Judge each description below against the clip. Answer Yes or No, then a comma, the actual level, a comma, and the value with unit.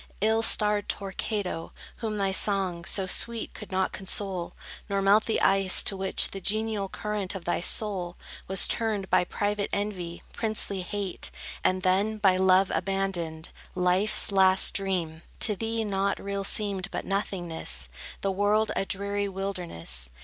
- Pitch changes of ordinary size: No, narrow, 1.9 semitones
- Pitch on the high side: Yes, high, 195 Hz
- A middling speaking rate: Yes, average, 150 wpm